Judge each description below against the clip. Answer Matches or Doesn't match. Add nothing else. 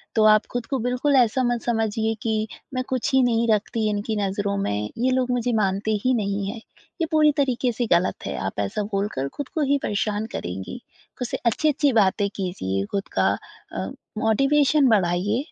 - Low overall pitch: Doesn't match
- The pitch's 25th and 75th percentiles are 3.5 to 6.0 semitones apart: Matches